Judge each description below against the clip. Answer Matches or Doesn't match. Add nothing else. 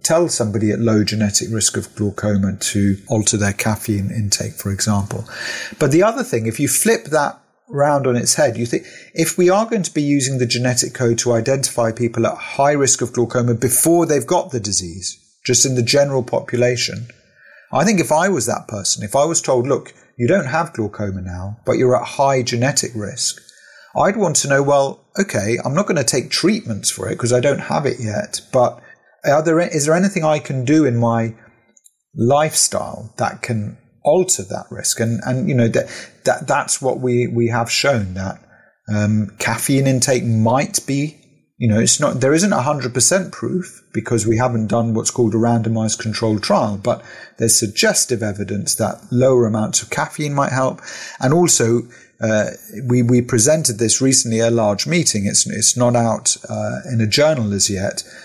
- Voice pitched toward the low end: Matches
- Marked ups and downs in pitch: Doesn't match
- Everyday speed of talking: Matches